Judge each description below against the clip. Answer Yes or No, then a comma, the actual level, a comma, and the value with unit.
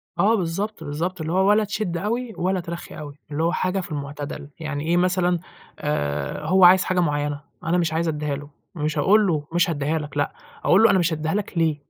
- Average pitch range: Yes, average, 3.8 semitones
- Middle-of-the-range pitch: Yes, medium, 165 Hz